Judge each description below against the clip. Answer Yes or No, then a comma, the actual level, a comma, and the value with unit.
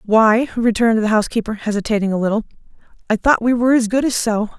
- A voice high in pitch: Yes, high, 225 Hz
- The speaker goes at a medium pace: Yes, average, 195 wpm